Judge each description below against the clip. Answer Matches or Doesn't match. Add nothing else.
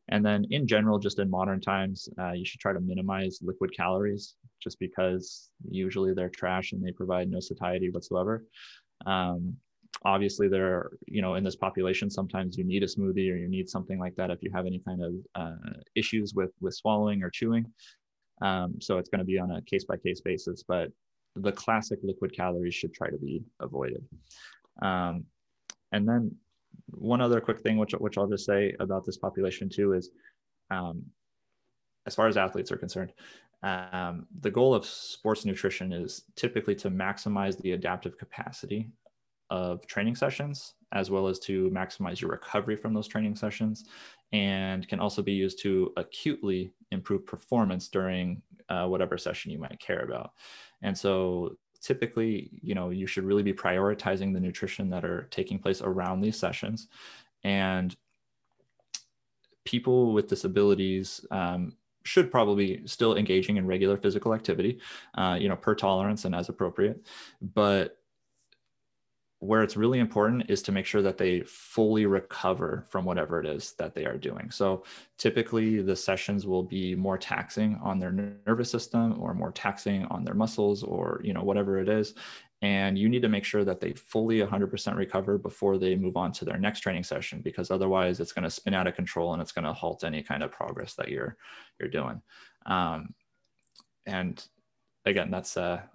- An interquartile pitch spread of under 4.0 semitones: Matches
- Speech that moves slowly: Doesn't match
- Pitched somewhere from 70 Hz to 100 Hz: Matches